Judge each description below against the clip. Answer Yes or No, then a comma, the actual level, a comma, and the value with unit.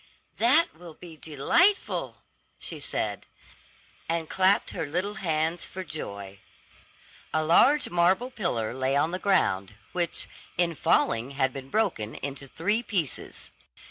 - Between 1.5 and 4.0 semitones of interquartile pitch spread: No, wide, 5.6 semitones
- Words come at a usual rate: No, slow, 130 wpm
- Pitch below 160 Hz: No, medium, 165 Hz